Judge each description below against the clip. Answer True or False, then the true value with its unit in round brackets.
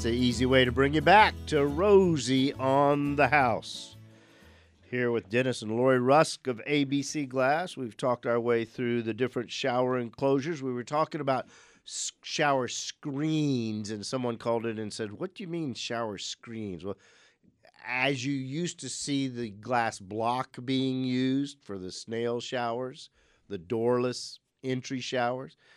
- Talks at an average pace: True (160 wpm)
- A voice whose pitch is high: False (125 Hz)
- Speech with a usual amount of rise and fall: True (3.1 semitones)